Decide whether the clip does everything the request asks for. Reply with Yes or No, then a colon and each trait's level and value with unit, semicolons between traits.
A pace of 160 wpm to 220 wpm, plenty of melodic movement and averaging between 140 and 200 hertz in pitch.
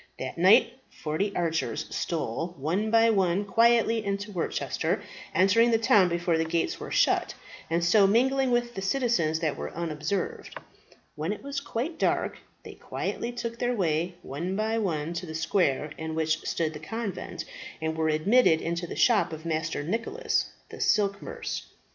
Yes: average, 170 wpm; wide, 5.9 semitones; medium, 185 Hz